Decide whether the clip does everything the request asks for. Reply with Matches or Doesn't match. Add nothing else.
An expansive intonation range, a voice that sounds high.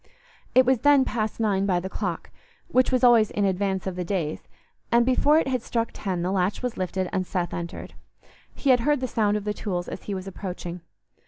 Doesn't match